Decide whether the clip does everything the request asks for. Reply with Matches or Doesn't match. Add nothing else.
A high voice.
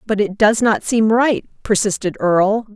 Matches